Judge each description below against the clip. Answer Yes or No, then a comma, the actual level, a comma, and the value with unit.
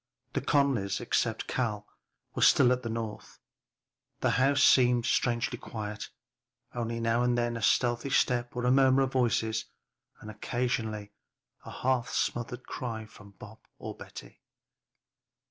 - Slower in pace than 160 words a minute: Yes, average, 140 wpm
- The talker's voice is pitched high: No, low, 120 Hz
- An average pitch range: No, narrow, 2.1 semitones